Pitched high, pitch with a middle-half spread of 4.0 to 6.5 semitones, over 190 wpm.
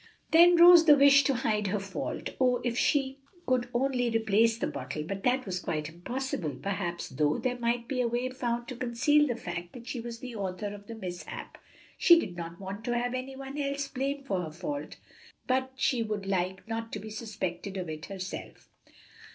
Yes: high, 235 Hz; average, 5.2 semitones; average, 200 wpm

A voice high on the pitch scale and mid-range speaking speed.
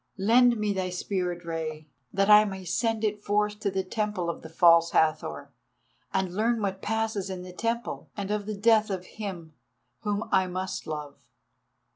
Yes: high, 195 Hz; average, 170 wpm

